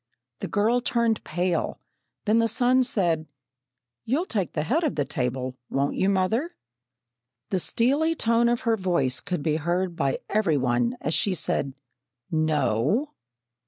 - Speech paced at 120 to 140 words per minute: No, average, 150 wpm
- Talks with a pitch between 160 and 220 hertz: Yes, medium, 185 Hz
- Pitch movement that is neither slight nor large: No, wide, 7.5 semitones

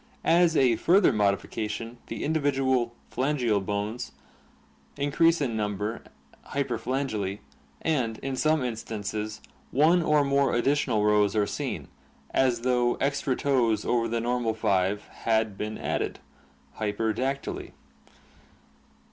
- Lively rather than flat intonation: No, average, 4.4 semitones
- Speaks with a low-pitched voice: Yes, low, 120 Hz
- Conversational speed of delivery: No, slow, 115 wpm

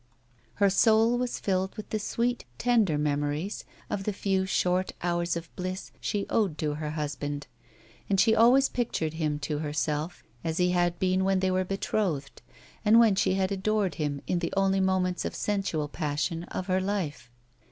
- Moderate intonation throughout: Yes, average, 4.2 semitones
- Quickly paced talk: No, average, 175 wpm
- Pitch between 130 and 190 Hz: Yes, medium, 185 Hz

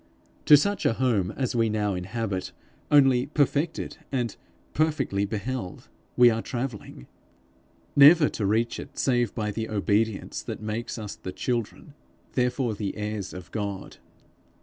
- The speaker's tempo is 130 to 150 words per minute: Yes, average, 140 wpm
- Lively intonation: No, average, 3.9 semitones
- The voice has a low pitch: Yes, low, 115 Hz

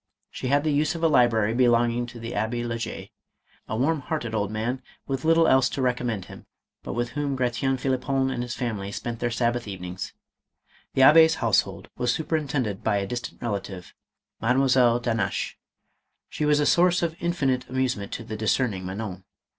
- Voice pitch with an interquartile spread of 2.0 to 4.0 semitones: Yes, average, 3.4 semitones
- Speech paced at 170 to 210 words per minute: Yes, average, 180 wpm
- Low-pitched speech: Yes, low, 120 Hz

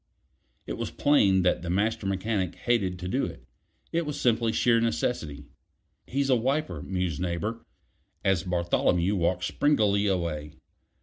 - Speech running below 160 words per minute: Yes, average, 140 wpm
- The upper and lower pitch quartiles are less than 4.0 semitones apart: No, average, 4.6 semitones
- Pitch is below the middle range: Yes, very low, 95 Hz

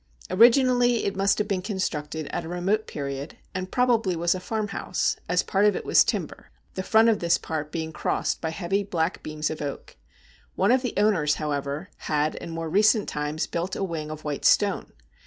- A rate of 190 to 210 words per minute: Yes, average, 195 wpm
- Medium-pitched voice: Yes, medium, 180 Hz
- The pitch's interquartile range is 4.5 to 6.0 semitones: Yes, average, 5.0 semitones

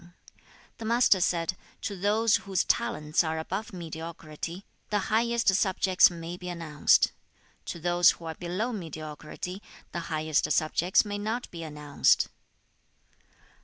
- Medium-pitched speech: Yes, medium, 175 Hz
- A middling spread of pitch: Yes, average, 4.1 semitones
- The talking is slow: Yes, slow, 130 wpm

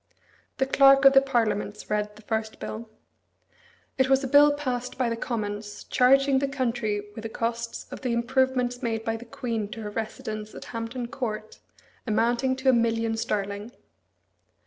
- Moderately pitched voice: No, high, 235 Hz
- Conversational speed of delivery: Yes, average, 170 wpm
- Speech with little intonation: No, average, 3.2 semitones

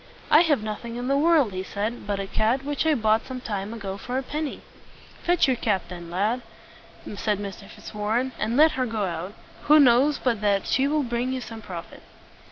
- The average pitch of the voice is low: No, high, 230 Hz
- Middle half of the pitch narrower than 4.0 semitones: No, average, 4.6 semitones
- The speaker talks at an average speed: No, fast, 210 wpm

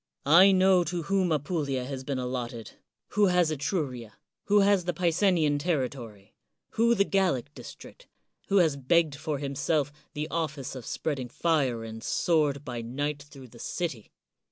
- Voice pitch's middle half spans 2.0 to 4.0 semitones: No, average, 5.1 semitones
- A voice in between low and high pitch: Yes, medium, 150 Hz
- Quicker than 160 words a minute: No, average, 150 wpm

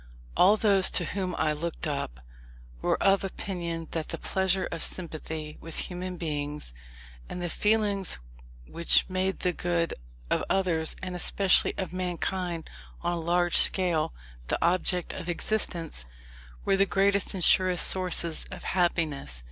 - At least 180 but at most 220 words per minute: No, average, 145 wpm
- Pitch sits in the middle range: Yes, medium, 175 Hz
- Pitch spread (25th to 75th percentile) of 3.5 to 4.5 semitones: No, narrow, 2.5 semitones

